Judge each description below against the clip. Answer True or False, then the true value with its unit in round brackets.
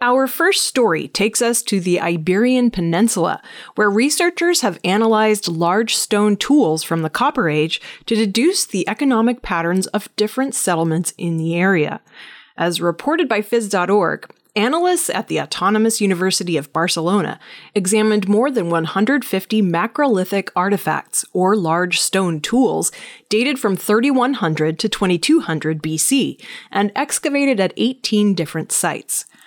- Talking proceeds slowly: True (130 wpm)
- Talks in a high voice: True (210 Hz)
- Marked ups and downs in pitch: True (5.7 semitones)